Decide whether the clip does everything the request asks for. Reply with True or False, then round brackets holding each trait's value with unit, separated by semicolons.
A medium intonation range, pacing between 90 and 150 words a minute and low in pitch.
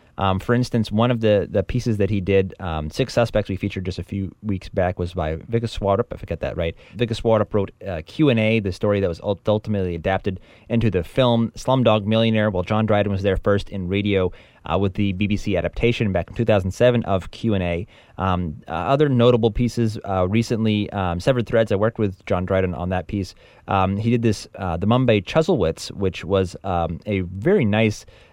False (3.2 semitones; 200 wpm; 100 Hz)